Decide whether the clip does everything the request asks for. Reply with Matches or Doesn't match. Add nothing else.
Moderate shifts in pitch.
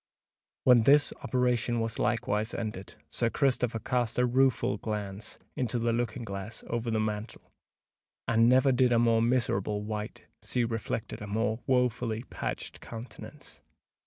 Doesn't match